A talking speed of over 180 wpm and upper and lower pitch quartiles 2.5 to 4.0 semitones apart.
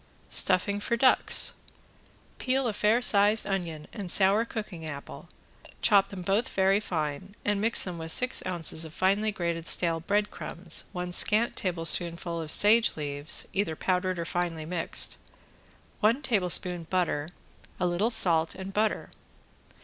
No: average, 140 wpm; average, 3.7 semitones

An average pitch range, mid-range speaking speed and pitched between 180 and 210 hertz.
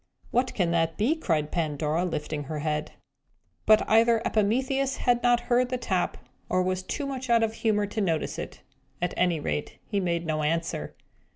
No: wide, 6.5 semitones; average, 180 wpm; medium, 185 Hz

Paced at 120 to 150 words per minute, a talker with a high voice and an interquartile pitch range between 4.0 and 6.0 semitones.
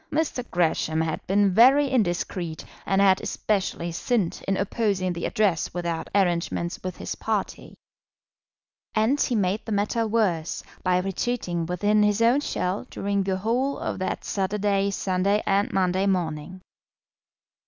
No: average, 140 wpm; high, 195 Hz; average, 3.0 semitones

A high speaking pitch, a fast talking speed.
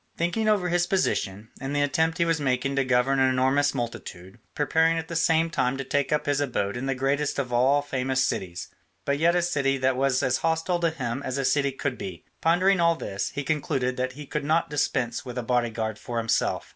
No: low, 135 Hz; fast, 220 wpm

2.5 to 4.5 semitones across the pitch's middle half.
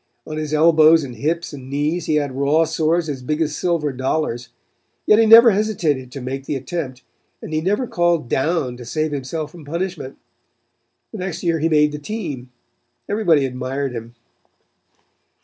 Yes: average, 4.0 semitones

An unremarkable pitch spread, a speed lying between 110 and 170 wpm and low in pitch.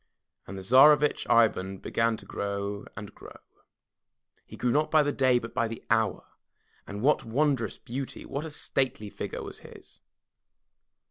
Yes: average, 5.0 semitones; average, 155 wpm; low, 115 Hz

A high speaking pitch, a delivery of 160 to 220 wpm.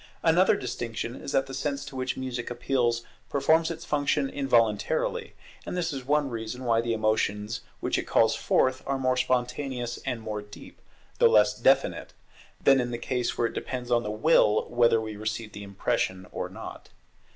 No: low, 125 Hz; average, 180 wpm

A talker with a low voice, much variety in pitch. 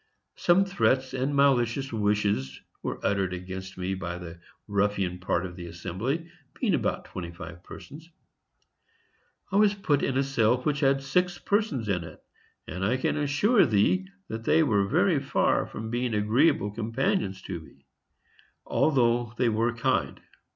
Yes: low, 115 Hz; wide, 6.7 semitones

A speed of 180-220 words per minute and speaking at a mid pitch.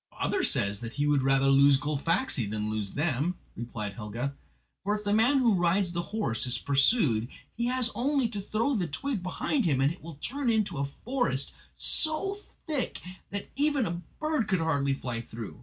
Yes: average, 190 wpm; medium, 170 Hz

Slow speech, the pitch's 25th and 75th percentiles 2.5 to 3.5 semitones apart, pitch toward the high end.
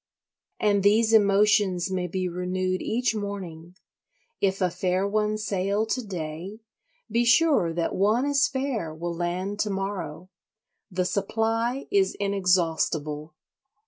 Yes: slow, 125 wpm; average, 3.2 semitones; high, 195 Hz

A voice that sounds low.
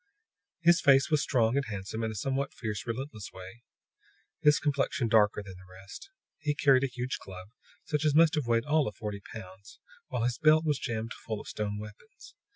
Yes: low, 120 Hz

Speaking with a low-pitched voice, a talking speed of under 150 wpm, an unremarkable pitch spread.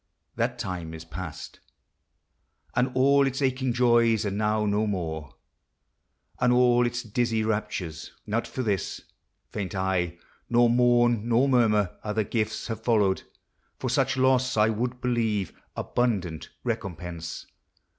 Yes: low, 110 Hz; slow, 135 wpm; average, 4.0 semitones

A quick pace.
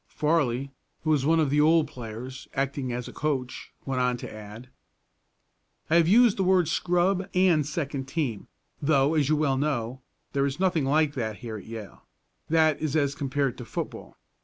No: average, 185 wpm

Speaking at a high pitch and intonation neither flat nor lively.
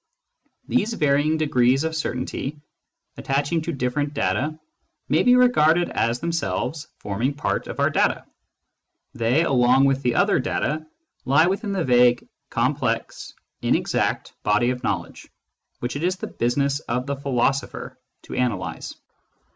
No: medium, 140 Hz; average, 4.2 semitones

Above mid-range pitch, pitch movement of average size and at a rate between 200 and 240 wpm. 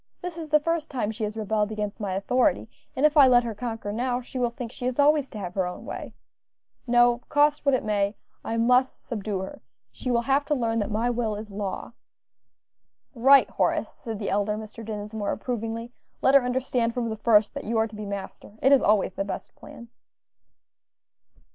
Yes: high, 230 Hz; average, 3.2 semitones; fast, 205 wpm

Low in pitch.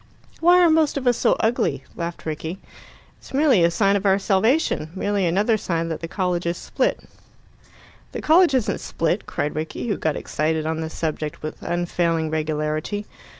No: medium, 175 Hz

